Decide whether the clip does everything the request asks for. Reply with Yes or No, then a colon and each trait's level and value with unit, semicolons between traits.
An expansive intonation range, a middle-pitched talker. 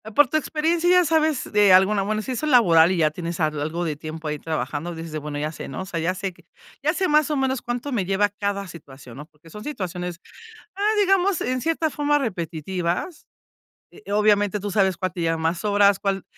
No: wide, 7.6 semitones; high, 195 Hz